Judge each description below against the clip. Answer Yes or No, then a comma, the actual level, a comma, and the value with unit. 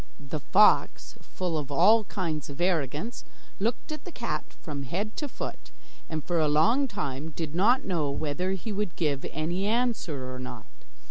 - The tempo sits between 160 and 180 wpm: Yes, average, 175 wpm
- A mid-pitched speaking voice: Yes, medium, 170 Hz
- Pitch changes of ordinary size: No, wide, 6.1 semitones